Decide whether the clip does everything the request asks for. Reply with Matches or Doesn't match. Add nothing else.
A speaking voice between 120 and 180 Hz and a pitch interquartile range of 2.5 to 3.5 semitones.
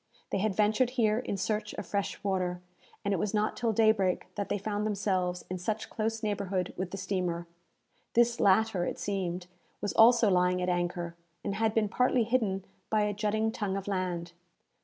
Doesn't match